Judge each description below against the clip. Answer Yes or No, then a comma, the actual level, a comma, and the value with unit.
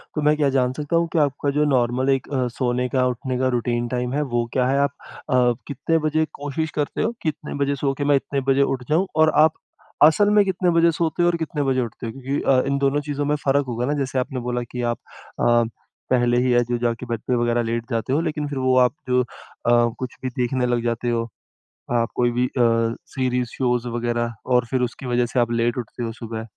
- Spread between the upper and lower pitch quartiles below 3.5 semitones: Yes, average, 3.0 semitones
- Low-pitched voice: Yes, low, 130 Hz